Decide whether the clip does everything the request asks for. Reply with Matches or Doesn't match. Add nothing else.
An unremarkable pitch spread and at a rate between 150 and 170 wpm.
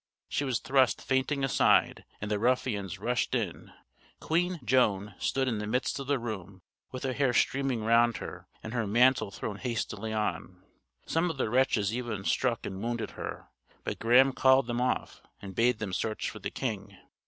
Doesn't match